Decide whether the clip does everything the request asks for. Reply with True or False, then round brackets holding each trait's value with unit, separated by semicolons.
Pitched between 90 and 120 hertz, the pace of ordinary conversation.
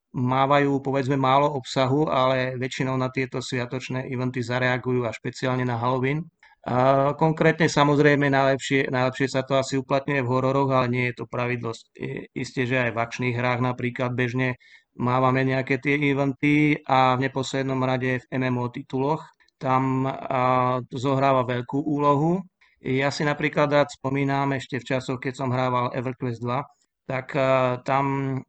False (130 Hz; 145 wpm)